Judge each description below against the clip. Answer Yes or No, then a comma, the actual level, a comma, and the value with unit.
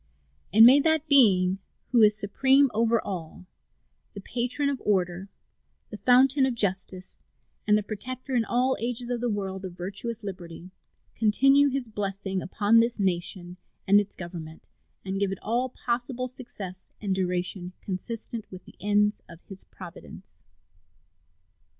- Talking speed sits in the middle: Yes, average, 145 wpm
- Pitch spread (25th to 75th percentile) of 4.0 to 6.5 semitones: Yes, average, 4.5 semitones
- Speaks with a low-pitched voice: No, high, 210 Hz